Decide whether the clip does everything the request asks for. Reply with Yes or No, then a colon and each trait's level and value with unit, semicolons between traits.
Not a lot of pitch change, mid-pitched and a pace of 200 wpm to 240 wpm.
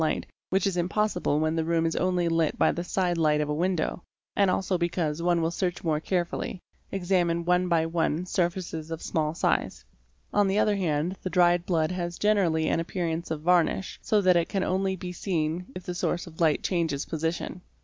Yes: narrow, 2.1 semitones; medium, 175 Hz; fast, 205 wpm